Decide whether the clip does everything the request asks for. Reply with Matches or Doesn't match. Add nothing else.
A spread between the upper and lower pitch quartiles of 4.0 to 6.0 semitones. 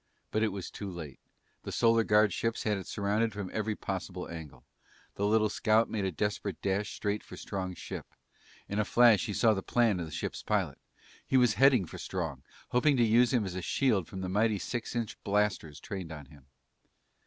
Doesn't match